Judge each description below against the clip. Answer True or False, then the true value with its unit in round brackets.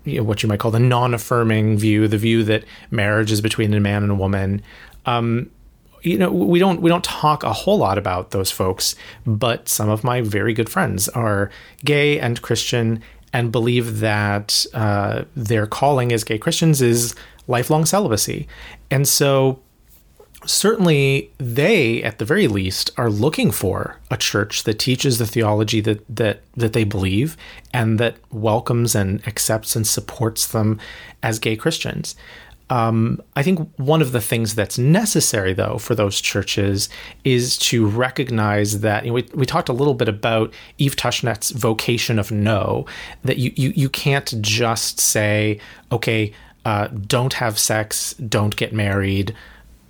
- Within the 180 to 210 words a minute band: False (160 wpm)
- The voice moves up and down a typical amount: True (3.3 semitones)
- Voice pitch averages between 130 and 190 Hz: False (115 Hz)